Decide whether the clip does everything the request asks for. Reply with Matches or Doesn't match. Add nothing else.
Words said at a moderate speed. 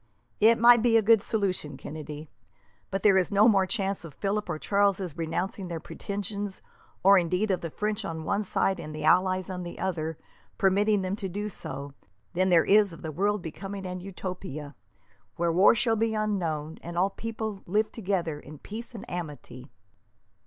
Matches